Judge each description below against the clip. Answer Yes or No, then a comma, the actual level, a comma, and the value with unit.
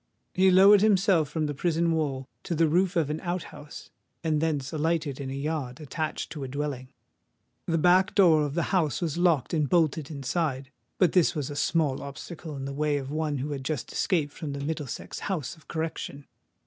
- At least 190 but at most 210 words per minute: Yes, average, 200 wpm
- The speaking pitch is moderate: Yes, medium, 155 Hz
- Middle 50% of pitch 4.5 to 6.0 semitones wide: No, average, 3.2 semitones